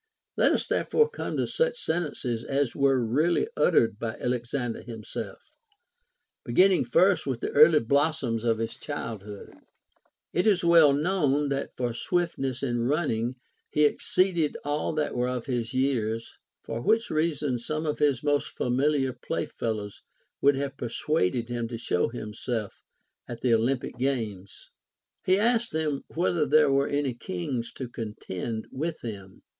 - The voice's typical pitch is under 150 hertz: Yes, low, 135 Hz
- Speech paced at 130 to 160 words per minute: Yes, average, 150 wpm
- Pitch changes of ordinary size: Yes, average, 4.6 semitones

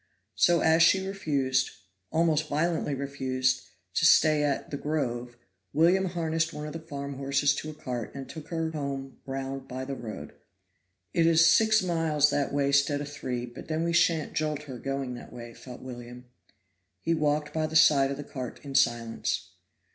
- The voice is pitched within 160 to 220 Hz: No, medium, 145 Hz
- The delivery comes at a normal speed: Yes, average, 180 wpm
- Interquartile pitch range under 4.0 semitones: Yes, average, 3.3 semitones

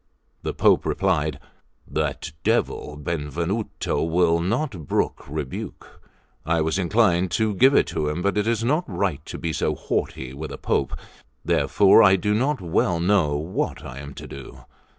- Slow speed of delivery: No, average, 160 wpm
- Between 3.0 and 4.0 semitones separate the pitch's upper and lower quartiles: No, average, 5.3 semitones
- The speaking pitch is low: Yes, very low, 85 Hz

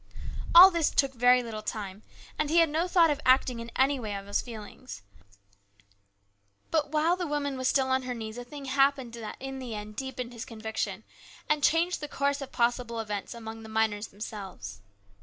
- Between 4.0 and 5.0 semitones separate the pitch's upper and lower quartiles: Yes, average, 4.4 semitones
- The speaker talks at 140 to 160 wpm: No, average, 195 wpm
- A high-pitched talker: Yes, very high, 250 Hz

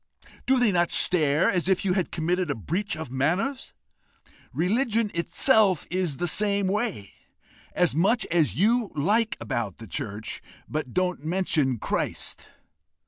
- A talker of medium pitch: Yes, medium, 180 Hz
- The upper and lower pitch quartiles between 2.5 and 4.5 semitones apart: No, average, 5.3 semitones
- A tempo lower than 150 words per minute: Yes, average, 140 wpm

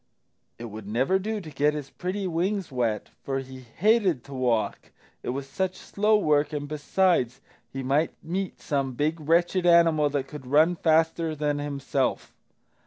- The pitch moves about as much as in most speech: Yes, average, 4.6 semitones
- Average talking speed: Yes, average, 165 wpm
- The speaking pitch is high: No, medium, 150 Hz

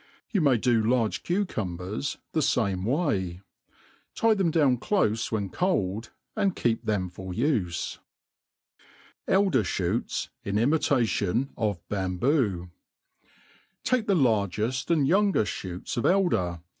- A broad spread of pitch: Yes, wide, 8.4 semitones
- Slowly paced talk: Yes, slow, 105 wpm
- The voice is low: Yes, low, 115 Hz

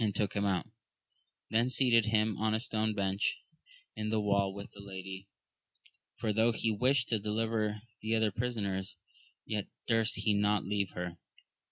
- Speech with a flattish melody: Yes, narrow, 1.9 semitones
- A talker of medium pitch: No, low, 105 Hz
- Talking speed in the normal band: Yes, average, 160 wpm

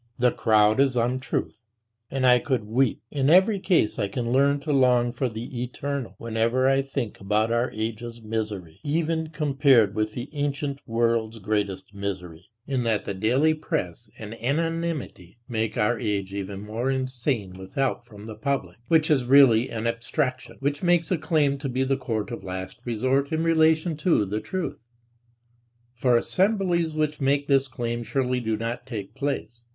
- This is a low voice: Yes, low, 125 Hz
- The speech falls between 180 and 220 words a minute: No, average, 170 wpm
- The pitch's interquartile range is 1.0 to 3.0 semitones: No, average, 4.3 semitones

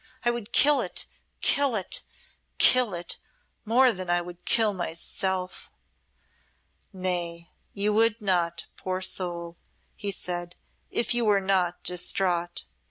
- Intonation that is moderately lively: Yes, average, 3.6 semitones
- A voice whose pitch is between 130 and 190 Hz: Yes, medium, 185 Hz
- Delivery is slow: Yes, slow, 125 wpm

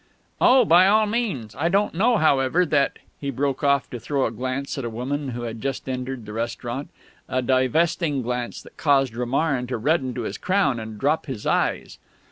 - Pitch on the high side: No, low, 135 Hz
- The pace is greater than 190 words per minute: Yes, average, 200 wpm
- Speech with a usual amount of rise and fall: Yes, average, 4.4 semitones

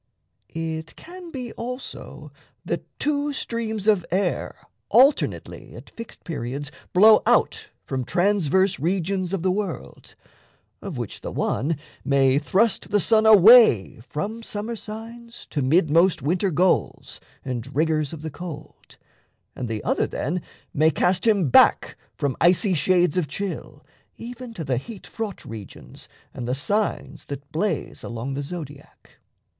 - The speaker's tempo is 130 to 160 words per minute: Yes, average, 140 wpm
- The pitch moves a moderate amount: No, wide, 6.9 semitones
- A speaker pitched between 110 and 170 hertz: No, medium, 180 Hz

